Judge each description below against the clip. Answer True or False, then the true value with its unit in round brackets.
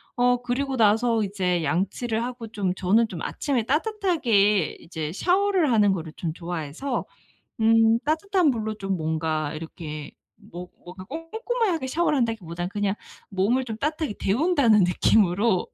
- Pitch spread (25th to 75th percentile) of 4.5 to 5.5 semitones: False (6.8 semitones)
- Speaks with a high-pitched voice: True (220 Hz)